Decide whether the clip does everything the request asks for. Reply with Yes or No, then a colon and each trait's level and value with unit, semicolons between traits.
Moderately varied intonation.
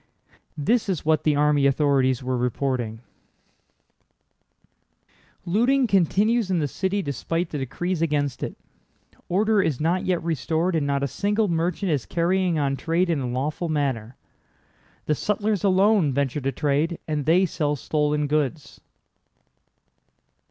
Yes: average, 4.7 semitones